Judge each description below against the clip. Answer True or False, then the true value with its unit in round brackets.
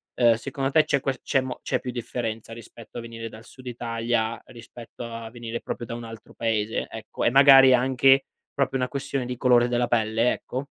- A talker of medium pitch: False (120 Hz)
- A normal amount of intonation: False (2.2 semitones)